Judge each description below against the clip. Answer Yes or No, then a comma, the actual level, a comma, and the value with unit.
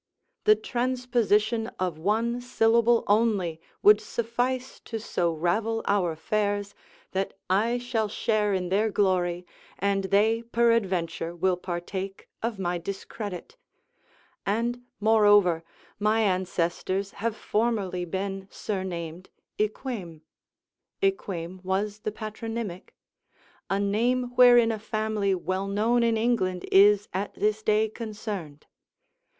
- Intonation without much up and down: No, average, 3.3 semitones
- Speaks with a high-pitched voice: Yes, high, 205 Hz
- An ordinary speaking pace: No, slow, 110 wpm